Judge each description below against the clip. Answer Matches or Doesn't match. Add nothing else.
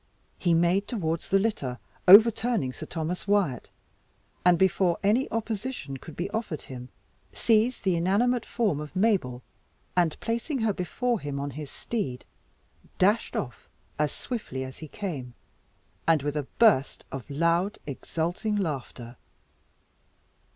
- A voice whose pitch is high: Doesn't match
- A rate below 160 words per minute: Matches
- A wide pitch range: Matches